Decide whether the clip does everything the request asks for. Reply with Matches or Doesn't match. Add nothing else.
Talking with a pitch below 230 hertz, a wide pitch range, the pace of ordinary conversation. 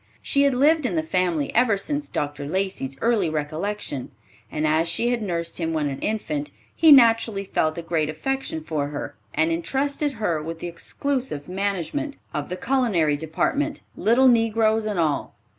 Matches